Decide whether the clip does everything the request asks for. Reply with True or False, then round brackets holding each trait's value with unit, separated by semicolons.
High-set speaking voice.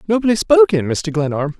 False (170 Hz)